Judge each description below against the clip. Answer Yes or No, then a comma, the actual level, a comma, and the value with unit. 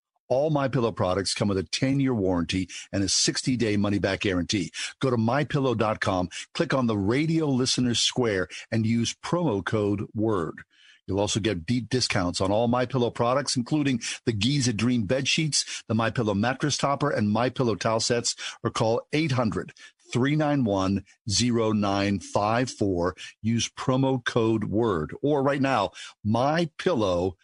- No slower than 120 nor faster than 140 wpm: Yes, slow, 135 wpm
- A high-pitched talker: No, low, 115 Hz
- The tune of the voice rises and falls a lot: No, average, 4.3 semitones